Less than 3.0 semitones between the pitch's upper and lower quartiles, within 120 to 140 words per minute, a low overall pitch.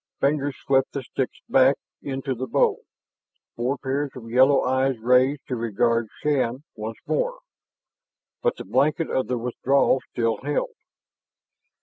Yes: narrow, 2.4 semitones; slow, 135 wpm; low, 130 Hz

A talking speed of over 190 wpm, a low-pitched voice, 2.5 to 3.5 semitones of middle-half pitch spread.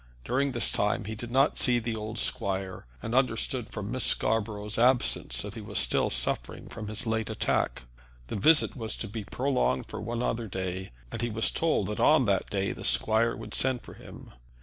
Yes: average, 200 wpm; low, 110 Hz; average, 2.9 semitones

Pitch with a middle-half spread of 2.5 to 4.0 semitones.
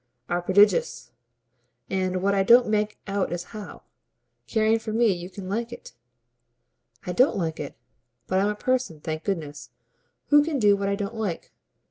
Yes: average, 3.4 semitones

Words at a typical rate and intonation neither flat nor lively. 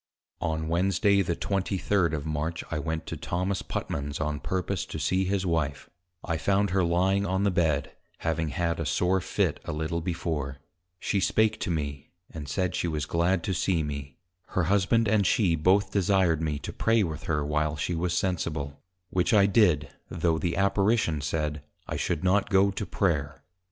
Yes: average, 180 wpm; average, 3.9 semitones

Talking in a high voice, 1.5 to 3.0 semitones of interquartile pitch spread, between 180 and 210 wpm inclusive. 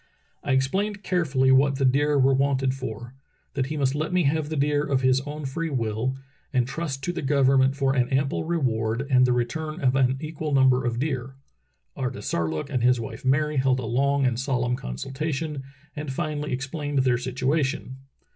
No: low, 135 Hz; narrow, 2.4 semitones; average, 185 wpm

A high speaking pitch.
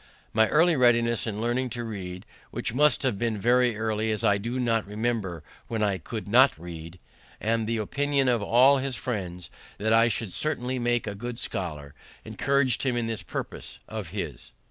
No: low, 115 Hz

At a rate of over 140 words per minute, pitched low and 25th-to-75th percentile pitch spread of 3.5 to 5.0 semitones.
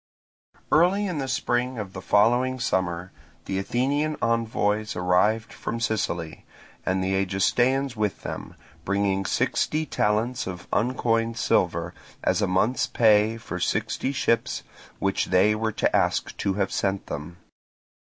No: slow, 135 wpm; low, 110 Hz; average, 4.3 semitones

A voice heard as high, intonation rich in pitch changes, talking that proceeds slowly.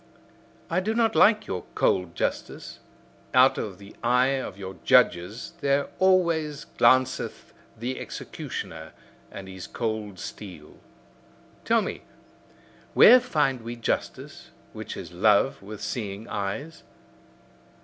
No: low, 115 Hz; wide, 6.9 semitones; slow, 120 wpm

